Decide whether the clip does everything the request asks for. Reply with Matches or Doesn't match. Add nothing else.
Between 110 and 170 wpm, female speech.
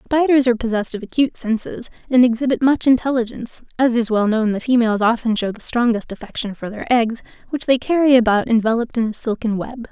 Doesn't match